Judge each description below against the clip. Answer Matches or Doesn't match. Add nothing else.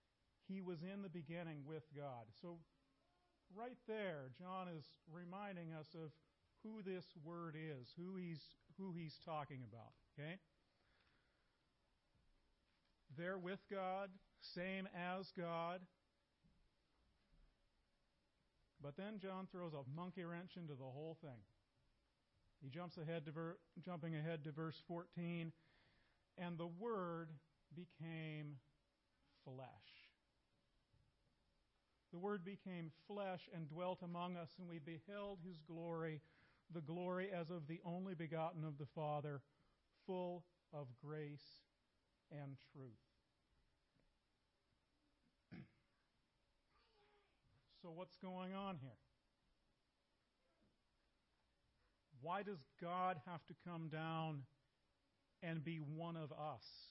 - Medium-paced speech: Doesn't match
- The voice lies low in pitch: Doesn't match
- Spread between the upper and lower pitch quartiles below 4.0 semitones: Matches